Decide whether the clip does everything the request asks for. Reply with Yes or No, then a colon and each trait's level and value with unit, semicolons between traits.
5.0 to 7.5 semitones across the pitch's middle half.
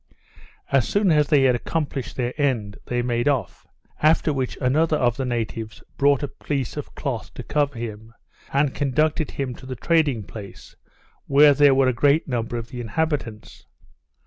No: average, 3.6 semitones